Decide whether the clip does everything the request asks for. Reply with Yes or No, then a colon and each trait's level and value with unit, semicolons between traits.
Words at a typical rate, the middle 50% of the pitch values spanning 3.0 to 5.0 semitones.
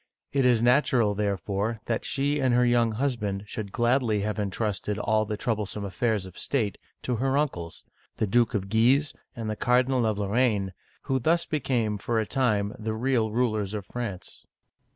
Yes: average, 170 wpm; average, 3.3 semitones